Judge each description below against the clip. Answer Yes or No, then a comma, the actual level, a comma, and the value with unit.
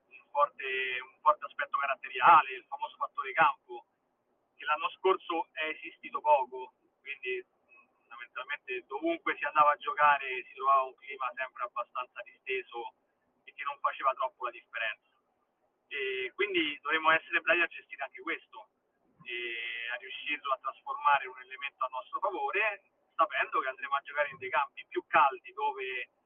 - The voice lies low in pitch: No, very high, 295 Hz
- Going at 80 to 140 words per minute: No, average, 155 wpm